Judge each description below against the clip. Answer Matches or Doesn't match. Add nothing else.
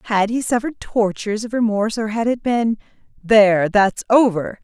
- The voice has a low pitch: Doesn't match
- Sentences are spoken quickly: Doesn't match